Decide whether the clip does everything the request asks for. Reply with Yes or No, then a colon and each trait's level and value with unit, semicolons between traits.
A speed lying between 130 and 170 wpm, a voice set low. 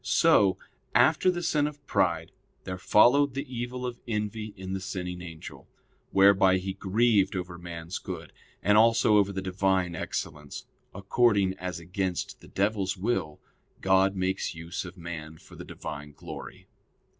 Yes: average, 150 wpm; very low, 95 Hz